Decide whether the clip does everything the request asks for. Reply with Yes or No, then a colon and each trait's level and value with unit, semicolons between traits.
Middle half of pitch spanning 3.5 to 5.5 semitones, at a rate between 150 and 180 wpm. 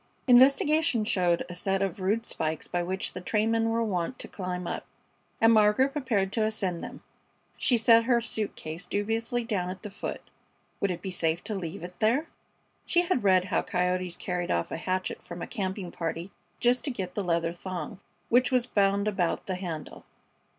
No: average, 4.2 semitones; average, 190 wpm